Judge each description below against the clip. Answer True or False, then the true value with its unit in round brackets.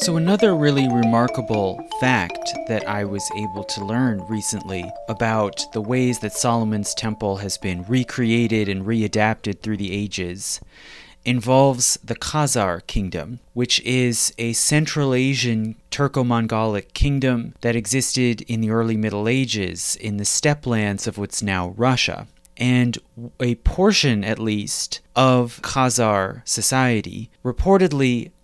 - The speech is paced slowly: True (130 wpm)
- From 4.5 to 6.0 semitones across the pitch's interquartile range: False (3.4 semitones)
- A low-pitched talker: True (115 Hz)